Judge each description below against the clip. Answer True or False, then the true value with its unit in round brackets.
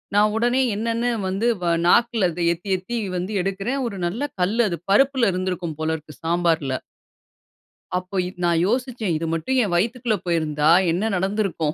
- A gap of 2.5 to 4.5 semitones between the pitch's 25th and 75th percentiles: False (5.2 semitones)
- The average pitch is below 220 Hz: True (190 Hz)